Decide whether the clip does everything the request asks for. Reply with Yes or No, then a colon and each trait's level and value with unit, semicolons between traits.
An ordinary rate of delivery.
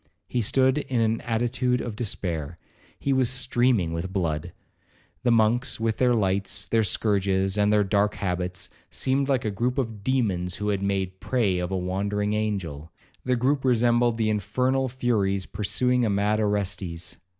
Yes: average, 155 wpm